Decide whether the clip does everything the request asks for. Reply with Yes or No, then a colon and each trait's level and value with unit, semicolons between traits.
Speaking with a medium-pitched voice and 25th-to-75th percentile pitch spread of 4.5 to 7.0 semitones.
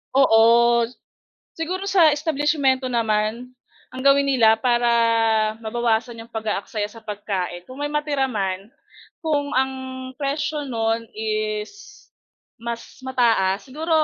No: very high, 255 Hz; average, 5.0 semitones